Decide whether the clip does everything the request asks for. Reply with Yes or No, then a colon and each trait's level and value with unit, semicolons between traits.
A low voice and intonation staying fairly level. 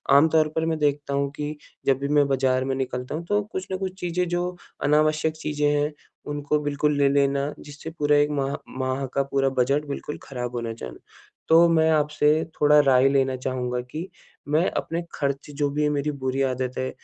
No: medium, 145 Hz; narrow, 2.1 semitones